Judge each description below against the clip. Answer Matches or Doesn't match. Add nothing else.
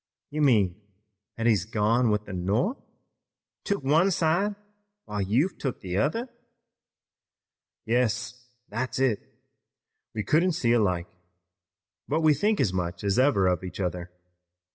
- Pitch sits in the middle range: Doesn't match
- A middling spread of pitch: Doesn't match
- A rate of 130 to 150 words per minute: Matches